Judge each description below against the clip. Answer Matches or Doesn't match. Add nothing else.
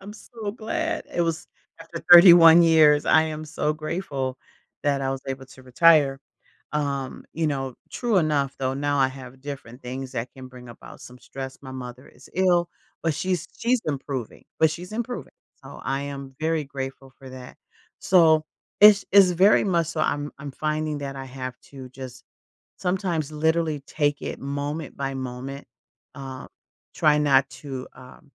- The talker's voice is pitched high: Doesn't match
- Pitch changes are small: Doesn't match